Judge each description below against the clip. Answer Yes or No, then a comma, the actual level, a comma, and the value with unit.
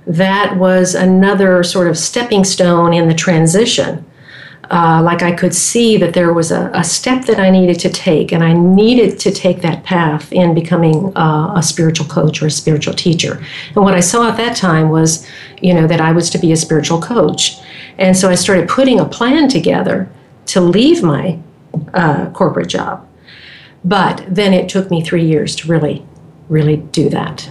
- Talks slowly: No, average, 190 wpm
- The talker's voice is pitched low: No, medium, 175 Hz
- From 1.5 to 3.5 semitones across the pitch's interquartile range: Yes, average, 2.9 semitones